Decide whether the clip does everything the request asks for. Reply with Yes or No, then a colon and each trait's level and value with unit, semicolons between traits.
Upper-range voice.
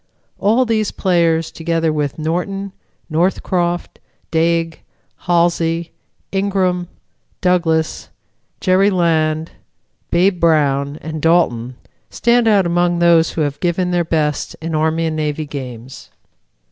No: medium, 165 Hz